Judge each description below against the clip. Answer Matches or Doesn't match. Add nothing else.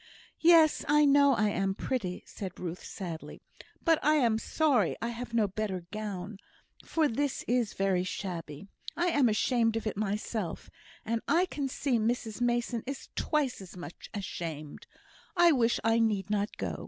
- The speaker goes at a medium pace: Matches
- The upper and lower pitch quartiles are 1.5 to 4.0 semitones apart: Doesn't match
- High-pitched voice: Matches